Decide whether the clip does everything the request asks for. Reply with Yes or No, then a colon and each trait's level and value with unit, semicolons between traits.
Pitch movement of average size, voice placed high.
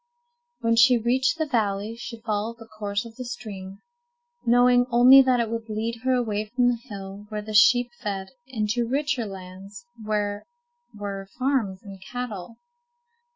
Yes: average, 3.1 semitones; high, 225 Hz